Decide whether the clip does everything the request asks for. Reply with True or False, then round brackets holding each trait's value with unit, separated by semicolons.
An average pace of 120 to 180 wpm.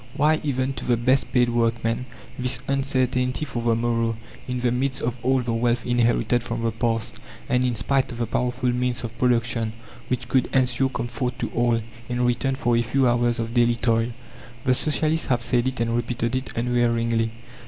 False (190 wpm)